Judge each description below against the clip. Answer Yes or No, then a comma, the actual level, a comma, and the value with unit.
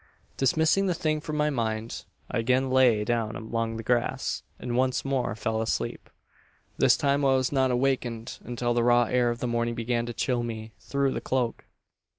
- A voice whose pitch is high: No, low, 120 Hz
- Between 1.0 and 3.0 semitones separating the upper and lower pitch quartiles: Yes, narrow, 2.4 semitones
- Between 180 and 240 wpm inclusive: Yes, average, 185 wpm